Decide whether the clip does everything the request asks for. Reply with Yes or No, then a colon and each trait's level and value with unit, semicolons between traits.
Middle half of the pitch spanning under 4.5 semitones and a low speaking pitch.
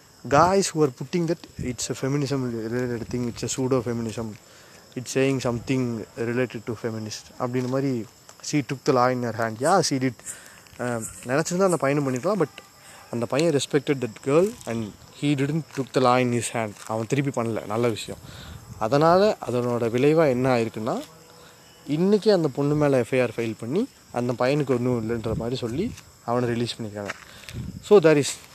Yes: average, 3.7 semitones; low, 125 Hz